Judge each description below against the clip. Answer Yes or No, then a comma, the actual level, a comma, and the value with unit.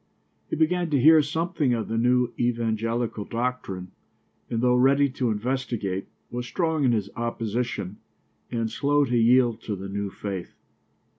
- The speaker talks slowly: No, average, 150 wpm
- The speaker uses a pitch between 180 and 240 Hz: No, low, 120 Hz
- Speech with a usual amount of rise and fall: Yes, average, 3.3 semitones